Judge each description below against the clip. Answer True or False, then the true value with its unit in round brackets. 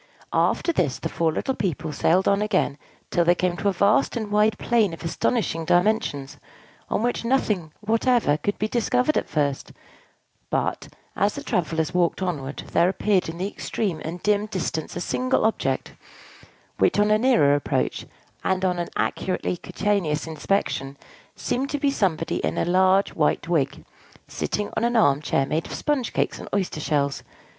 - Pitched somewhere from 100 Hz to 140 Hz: False (185 Hz)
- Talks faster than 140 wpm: True (170 wpm)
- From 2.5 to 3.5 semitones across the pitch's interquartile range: False (5.0 semitones)